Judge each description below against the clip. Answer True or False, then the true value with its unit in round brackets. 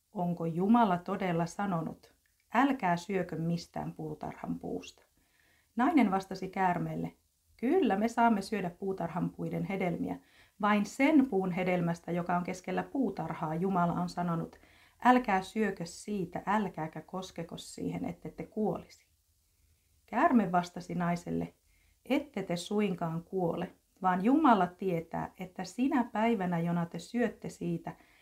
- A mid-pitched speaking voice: True (180 Hz)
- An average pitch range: True (3.7 semitones)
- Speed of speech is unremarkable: True (120 wpm)